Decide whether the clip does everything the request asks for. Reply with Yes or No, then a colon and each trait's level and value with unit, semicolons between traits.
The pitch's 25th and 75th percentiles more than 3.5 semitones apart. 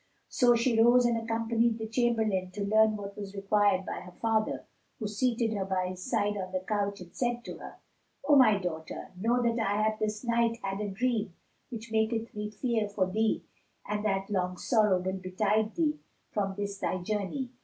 No: average, 2.7 semitones